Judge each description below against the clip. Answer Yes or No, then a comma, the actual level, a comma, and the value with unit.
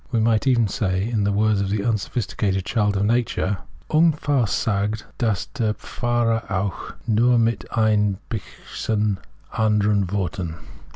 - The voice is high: No, low, 105 Hz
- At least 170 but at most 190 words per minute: No, slow, 135 wpm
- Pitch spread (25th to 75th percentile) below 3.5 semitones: Yes, narrow, 2.5 semitones